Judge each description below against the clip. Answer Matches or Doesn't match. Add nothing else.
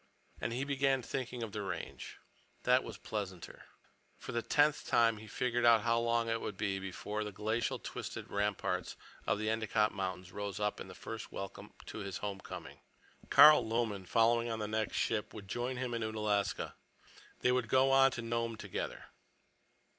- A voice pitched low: Matches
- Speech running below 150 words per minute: Doesn't match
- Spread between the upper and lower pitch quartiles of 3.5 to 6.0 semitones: Doesn't match